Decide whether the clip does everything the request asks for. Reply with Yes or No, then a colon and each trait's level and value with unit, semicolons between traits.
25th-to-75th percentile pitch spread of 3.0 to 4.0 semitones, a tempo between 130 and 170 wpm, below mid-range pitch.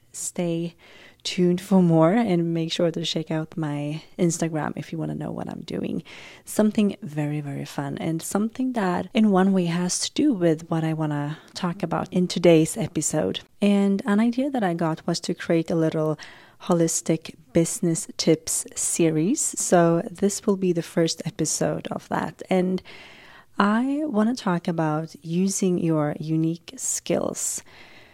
No: average, 3.5 semitones; average, 165 wpm; medium, 170 Hz